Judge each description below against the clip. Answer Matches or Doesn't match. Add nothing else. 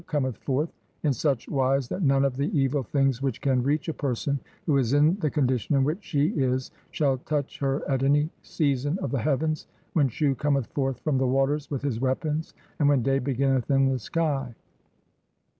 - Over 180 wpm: Matches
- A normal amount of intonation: Doesn't match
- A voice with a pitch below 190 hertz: Matches